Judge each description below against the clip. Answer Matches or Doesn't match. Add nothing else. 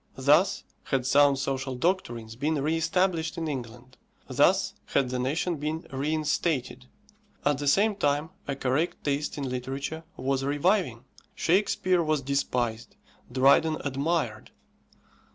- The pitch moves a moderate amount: Matches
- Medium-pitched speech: Matches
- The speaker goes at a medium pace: Doesn't match